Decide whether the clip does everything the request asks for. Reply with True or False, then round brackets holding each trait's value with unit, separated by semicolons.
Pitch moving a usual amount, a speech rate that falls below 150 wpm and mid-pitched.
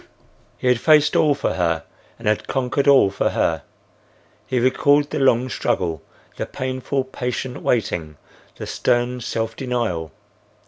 False (4.4 semitones; 140 wpm; 125 Hz)